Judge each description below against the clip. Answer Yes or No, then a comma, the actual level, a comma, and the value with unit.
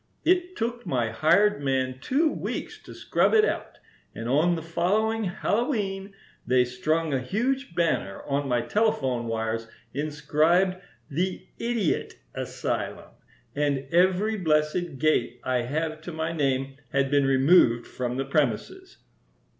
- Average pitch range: No, wide, 6.5 semitones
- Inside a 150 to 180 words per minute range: No, slow, 135 wpm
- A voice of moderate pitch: Yes, medium, 155 Hz